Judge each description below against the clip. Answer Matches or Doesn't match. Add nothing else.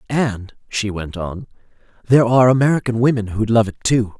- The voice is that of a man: Matches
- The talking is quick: Doesn't match